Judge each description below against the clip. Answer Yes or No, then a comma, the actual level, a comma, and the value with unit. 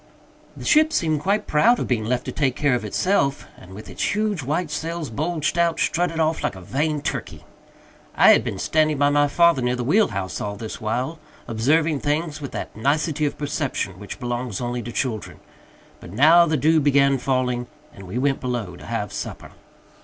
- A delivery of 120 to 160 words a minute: No, average, 200 wpm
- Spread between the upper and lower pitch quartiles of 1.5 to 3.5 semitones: No, average, 4.6 semitones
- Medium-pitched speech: Yes, medium, 145 Hz